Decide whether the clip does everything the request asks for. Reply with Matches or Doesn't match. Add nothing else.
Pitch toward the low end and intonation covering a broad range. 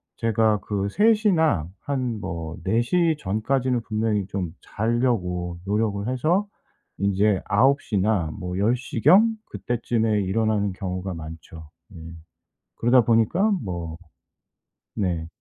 Doesn't match